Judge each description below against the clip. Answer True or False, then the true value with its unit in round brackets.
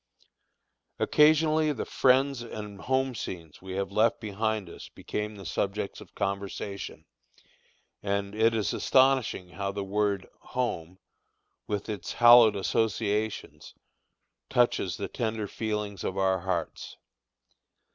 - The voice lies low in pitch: True (105 Hz)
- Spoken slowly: True (115 wpm)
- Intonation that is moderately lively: True (3.1 semitones)